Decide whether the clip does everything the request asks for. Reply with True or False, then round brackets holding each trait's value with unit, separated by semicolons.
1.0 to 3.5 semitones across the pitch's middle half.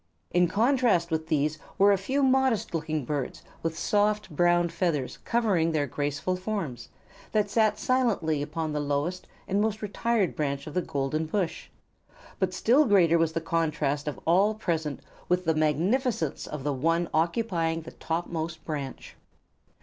False (4.9 semitones)